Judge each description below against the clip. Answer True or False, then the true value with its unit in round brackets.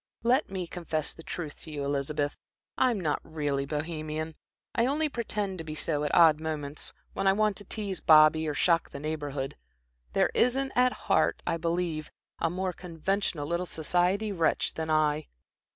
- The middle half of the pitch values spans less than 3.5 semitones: False (4.0 semitones)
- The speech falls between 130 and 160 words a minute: False (170 wpm)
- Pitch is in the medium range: True (160 Hz)